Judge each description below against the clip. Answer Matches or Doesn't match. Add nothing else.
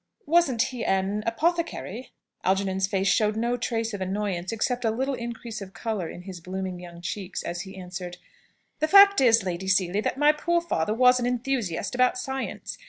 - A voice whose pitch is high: Matches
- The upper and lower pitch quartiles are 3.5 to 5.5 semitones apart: Matches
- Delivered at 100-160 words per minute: Doesn't match